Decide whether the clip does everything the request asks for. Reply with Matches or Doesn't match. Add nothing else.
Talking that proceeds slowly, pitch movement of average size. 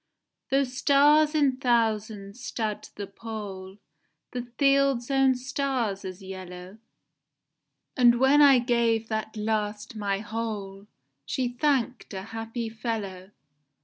Matches